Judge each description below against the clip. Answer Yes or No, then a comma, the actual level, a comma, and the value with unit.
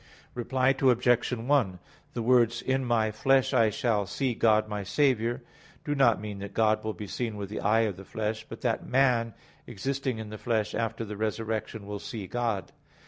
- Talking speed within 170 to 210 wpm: Yes, average, 190 wpm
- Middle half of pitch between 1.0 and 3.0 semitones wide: Yes, average, 2.7 semitones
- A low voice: Yes, low, 115 Hz